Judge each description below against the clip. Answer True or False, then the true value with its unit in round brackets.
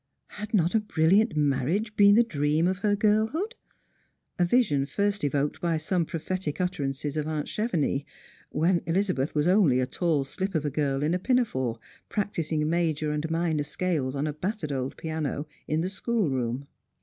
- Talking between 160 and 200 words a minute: True (175 wpm)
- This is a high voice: False (160 Hz)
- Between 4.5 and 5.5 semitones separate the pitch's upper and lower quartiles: True (5.2 semitones)